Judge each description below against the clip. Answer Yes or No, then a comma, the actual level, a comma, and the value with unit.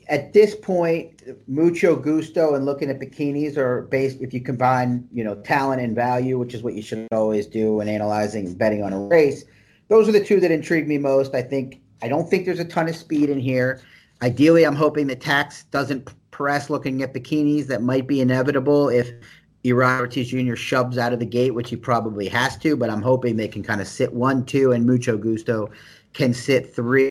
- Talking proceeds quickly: Yes, fast, 215 wpm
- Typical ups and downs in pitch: Yes, average, 3.3 semitones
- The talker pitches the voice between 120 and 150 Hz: Yes, low, 130 Hz